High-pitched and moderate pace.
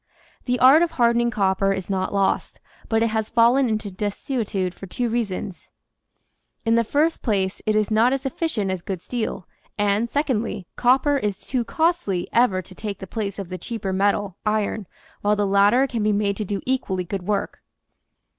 Yes: high, 210 Hz; average, 185 wpm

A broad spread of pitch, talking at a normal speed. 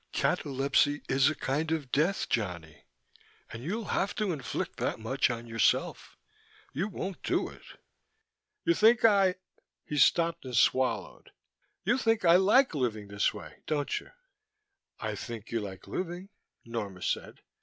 Yes: wide, 8.2 semitones; average, 150 wpm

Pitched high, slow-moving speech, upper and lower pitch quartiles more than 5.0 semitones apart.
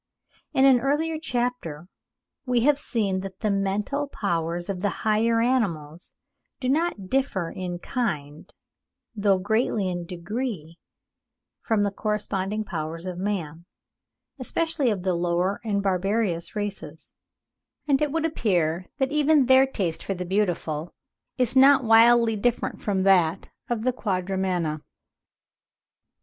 Yes: high, 205 Hz; slow, 130 wpm; wide, 5.6 semitones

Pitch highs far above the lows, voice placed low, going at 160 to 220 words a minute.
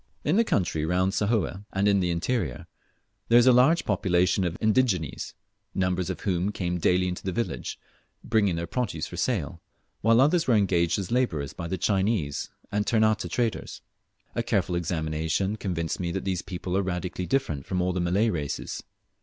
No: average, 3.9 semitones; very low, 95 Hz; average, 180 wpm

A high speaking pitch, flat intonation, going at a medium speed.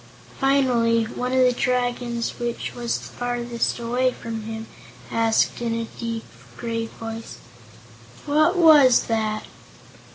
No: high, 235 Hz; narrow, 1.7 semitones; slow, 120 wpm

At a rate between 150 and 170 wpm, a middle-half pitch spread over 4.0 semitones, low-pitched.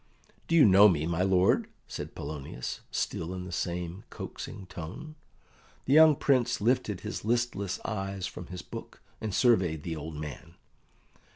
Yes: average, 155 wpm; average, 4.5 semitones; very low, 95 Hz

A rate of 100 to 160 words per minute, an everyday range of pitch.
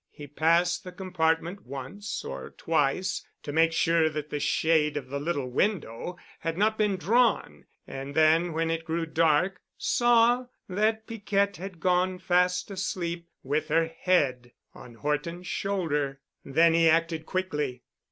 Yes: average, 145 wpm; average, 3.8 semitones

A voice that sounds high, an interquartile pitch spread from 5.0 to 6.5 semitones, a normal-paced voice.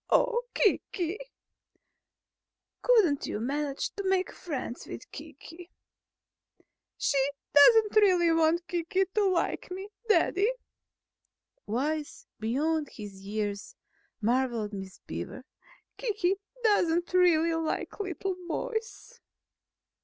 No: very high, 335 Hz; wide, 5.9 semitones; slow, 95 wpm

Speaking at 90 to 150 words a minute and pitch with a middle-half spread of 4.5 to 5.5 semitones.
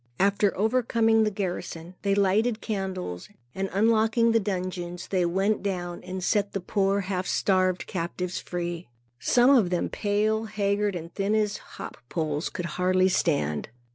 No: average, 145 wpm; average, 2.9 semitones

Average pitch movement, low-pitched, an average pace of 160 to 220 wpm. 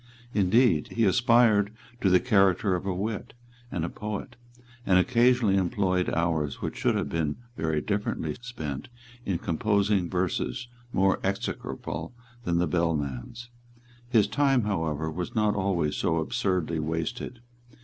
No: average, 4.8 semitones; very low, 95 Hz; slow, 135 wpm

